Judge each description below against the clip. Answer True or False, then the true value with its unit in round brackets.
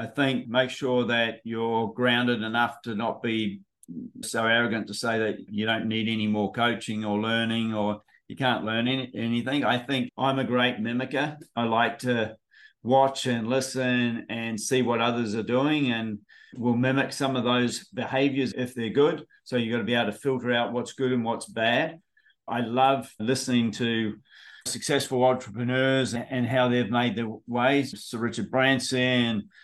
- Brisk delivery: False (175 wpm)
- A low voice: True (120 Hz)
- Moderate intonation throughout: False (2.3 semitones)